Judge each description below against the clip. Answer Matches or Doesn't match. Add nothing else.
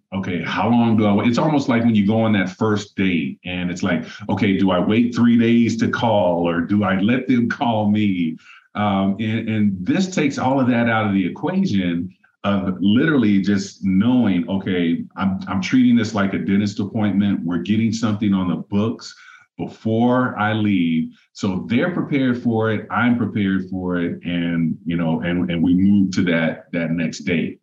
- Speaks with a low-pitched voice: Matches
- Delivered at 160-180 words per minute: Doesn't match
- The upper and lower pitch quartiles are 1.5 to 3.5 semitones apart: Doesn't match